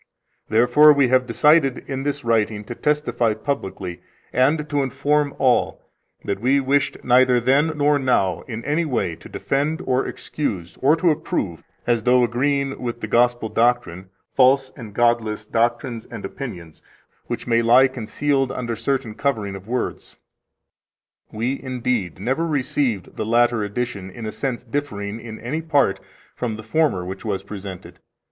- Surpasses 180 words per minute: No, average, 155 wpm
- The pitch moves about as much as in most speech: Yes, average, 4.1 semitones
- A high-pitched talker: No, low, 125 Hz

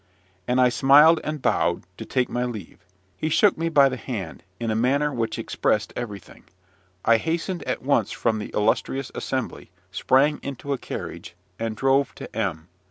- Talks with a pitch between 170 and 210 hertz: No, low, 125 Hz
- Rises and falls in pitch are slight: No, average, 4.2 semitones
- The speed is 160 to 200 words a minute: Yes, average, 170 wpm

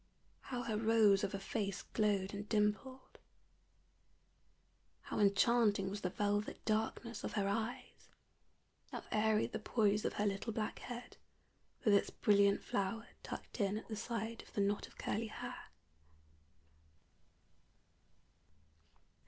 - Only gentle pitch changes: Yes, narrow, 2.1 semitones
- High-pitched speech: Yes, high, 210 Hz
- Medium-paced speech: No, slow, 130 wpm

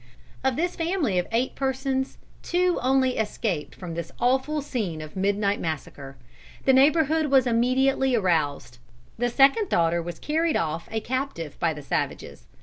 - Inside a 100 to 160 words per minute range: Yes, average, 150 wpm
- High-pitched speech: Yes, high, 245 Hz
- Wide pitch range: Yes, wide, 8.1 semitones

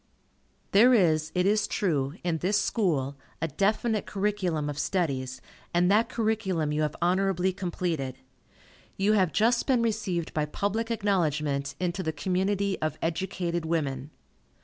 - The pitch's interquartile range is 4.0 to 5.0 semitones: Yes, average, 4.7 semitones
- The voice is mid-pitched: Yes, medium, 180 Hz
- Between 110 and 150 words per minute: Yes, average, 140 wpm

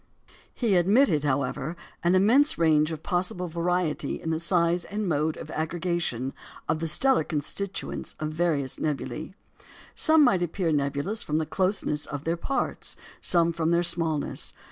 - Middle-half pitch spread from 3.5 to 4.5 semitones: No, average, 3.0 semitones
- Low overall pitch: No, medium, 170 Hz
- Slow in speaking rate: No, average, 150 wpm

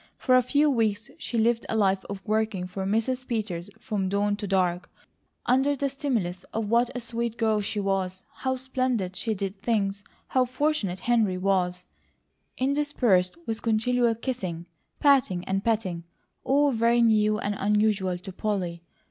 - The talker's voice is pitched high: Yes, high, 215 Hz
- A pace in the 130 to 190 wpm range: Yes, average, 155 wpm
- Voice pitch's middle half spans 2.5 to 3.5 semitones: No, average, 4.2 semitones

